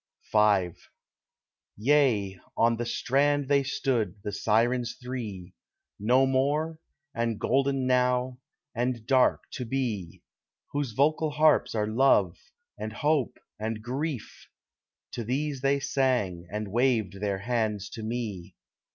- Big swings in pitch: No, average, 4.1 semitones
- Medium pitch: No, low, 120 Hz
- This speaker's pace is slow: Yes, slow, 120 wpm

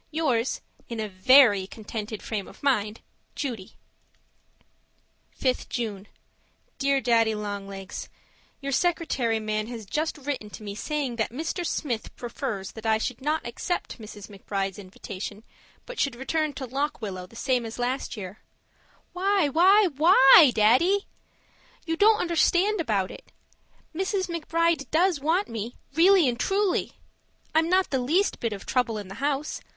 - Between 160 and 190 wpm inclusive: No, average, 150 wpm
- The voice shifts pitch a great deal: Yes, wide, 7.0 semitones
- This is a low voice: No, very high, 255 Hz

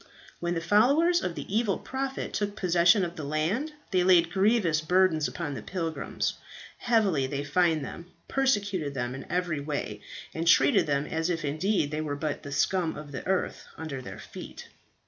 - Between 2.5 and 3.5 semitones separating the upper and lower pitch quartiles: No, average, 4.5 semitones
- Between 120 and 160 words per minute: No, average, 180 wpm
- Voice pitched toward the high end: No, medium, 170 Hz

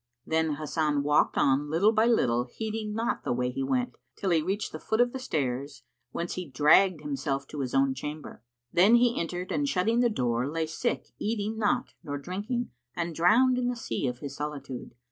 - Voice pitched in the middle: Yes, medium, 160 Hz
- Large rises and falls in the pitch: Yes, wide, 7.8 semitones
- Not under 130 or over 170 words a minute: No, average, 200 wpm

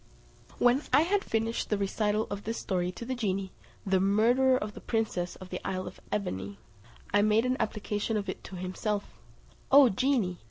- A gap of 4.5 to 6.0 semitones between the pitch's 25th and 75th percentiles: No, average, 3.6 semitones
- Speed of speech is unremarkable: Yes, average, 185 wpm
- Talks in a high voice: Yes, high, 210 Hz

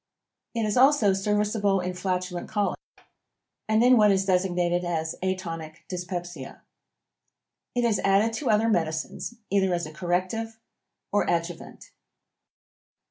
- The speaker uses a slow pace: Yes, slow, 125 wpm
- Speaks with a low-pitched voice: No, high, 190 Hz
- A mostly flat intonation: No, average, 3.2 semitones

